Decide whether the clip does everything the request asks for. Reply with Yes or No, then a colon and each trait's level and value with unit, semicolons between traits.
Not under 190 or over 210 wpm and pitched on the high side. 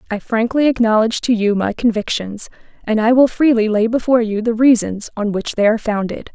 Yes: average, 200 wpm; high, 225 Hz